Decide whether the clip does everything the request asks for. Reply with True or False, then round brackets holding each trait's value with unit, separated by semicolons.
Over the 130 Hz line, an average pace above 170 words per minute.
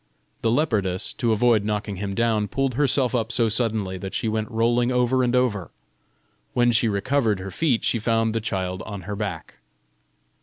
False (115 Hz; 180 wpm)